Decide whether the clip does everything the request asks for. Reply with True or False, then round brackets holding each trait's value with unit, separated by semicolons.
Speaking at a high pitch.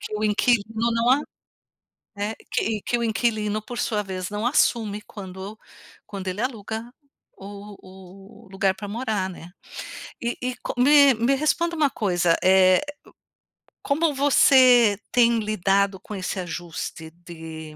True (210 Hz)